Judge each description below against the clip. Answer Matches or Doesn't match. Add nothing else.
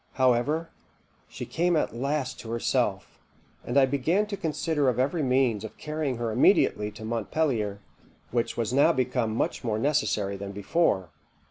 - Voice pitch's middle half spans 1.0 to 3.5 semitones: Doesn't match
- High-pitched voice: Doesn't match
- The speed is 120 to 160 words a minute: Matches